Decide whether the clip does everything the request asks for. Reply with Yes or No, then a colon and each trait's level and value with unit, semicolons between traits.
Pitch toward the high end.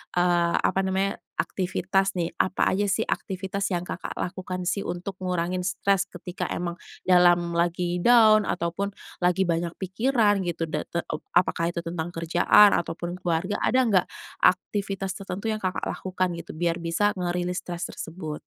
No: medium, 180 Hz